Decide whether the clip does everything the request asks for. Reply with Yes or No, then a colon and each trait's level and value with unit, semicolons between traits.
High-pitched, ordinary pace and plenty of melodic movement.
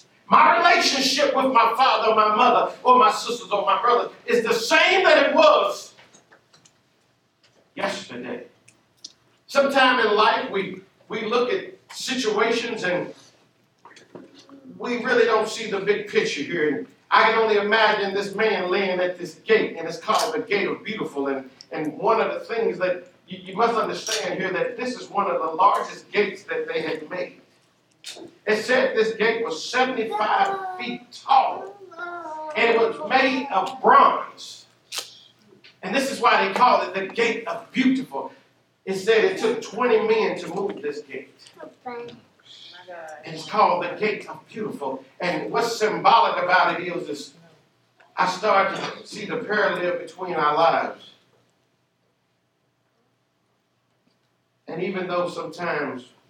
Yes: high, 220 Hz; average, 150 wpm; wide, 6.4 semitones